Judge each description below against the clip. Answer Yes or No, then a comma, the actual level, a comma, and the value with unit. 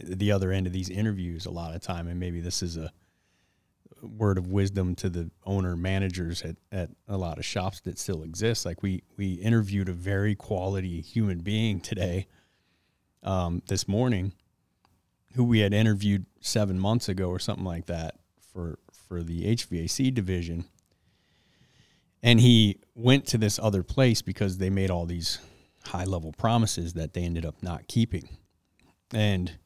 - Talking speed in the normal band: Yes, average, 165 wpm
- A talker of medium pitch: No, very low, 95 Hz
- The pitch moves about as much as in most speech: Yes, average, 3.0 semitones